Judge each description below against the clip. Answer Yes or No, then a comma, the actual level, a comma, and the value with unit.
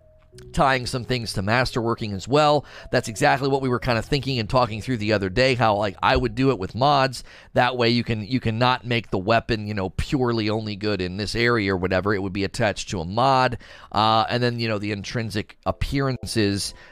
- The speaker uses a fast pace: Yes, fast, 225 wpm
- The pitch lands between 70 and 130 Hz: Yes, low, 115 Hz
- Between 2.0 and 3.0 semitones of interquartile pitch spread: No, average, 3.4 semitones